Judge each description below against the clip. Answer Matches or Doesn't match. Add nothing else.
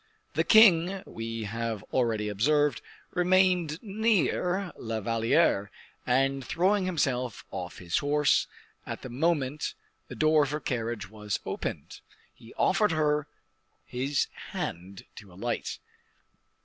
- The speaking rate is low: Matches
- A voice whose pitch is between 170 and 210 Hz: Doesn't match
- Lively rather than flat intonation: Matches